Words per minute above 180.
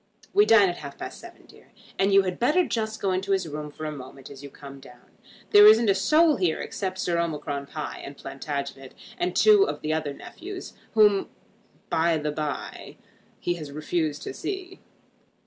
Yes: average, 190 wpm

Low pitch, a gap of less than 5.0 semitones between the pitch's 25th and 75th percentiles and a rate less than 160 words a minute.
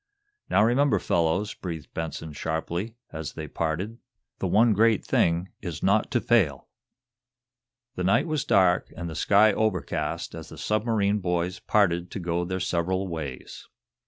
Yes: very low, 95 Hz; average, 4.0 semitones; average, 150 wpm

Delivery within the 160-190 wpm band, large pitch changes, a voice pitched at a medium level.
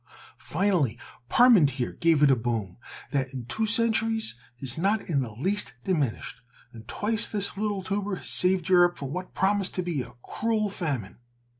Yes: average, 165 wpm; wide, 7.4 semitones; medium, 180 Hz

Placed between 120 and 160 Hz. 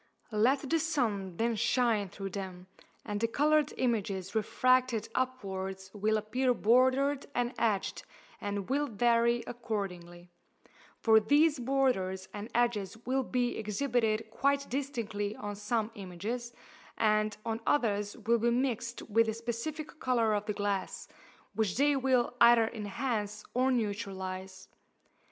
No: high, 225 Hz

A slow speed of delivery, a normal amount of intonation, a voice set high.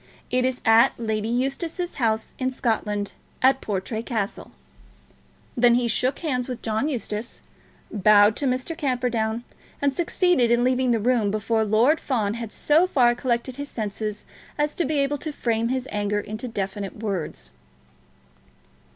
No: average, 150 wpm; average, 3.3 semitones; high, 240 Hz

